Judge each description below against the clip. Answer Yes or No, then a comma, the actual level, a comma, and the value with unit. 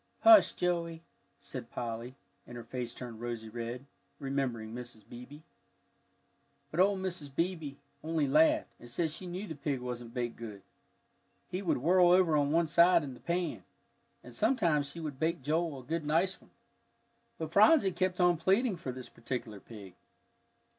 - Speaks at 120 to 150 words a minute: No, average, 165 wpm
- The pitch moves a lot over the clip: Yes, wide, 6.2 semitones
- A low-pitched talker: No, medium, 150 Hz